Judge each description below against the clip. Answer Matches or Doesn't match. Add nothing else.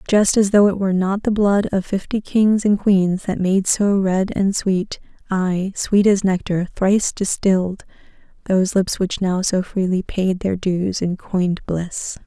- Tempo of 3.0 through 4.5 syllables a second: Matches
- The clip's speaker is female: Matches